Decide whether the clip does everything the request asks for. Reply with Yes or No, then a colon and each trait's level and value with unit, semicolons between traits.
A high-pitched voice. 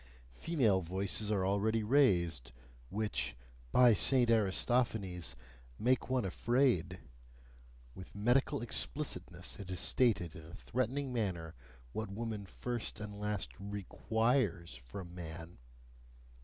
No: low, 105 Hz